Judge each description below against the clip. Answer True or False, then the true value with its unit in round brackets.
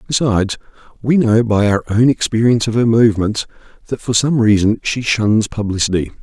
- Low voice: True (110 Hz)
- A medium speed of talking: True (165 wpm)